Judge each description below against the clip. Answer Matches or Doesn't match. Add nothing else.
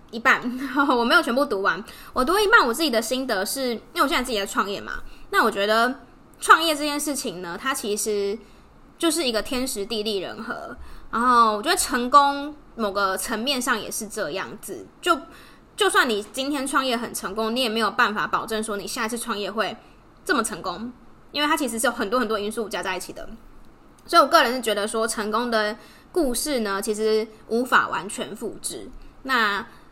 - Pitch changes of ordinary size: Matches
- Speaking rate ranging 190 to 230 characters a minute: Doesn't match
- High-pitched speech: Matches